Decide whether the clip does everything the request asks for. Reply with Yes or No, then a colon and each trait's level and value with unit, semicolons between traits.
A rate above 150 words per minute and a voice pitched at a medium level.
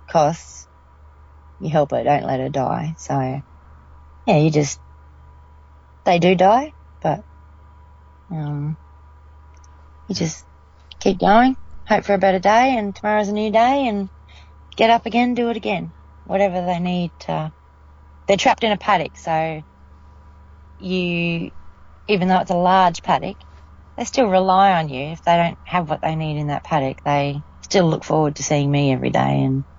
Yes: average, 160 wpm; medium, 145 Hz